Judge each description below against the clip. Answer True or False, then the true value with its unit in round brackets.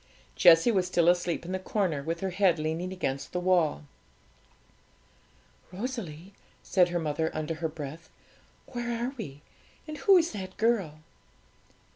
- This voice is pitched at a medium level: True (180 Hz)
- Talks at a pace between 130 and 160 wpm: True (145 wpm)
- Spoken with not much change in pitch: False (4.2 semitones)